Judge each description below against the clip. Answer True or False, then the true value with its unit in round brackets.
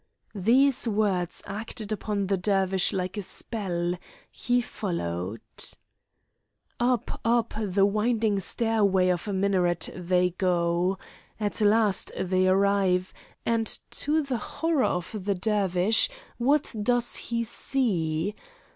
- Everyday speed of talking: False (115 wpm)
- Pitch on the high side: True (200 Hz)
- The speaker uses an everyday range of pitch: True (3.7 semitones)